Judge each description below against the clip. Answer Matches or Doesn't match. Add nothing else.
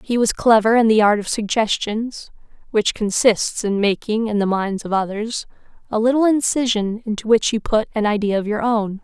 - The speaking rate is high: Doesn't match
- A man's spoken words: Doesn't match